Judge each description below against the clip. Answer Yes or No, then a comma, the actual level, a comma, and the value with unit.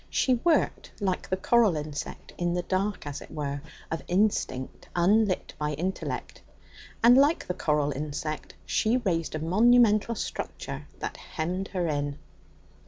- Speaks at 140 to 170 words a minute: Yes, average, 145 wpm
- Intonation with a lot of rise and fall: Yes, wide, 5.9 semitones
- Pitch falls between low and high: Yes, medium, 180 Hz